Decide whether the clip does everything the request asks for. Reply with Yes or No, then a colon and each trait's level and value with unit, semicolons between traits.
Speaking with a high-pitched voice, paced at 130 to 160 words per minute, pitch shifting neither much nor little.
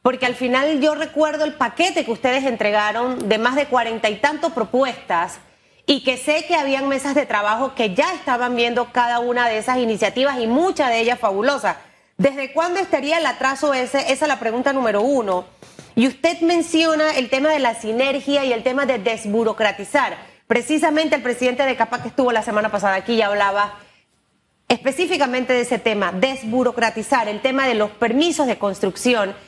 No: very high, 255 Hz; average, 180 wpm; average, 3.9 semitones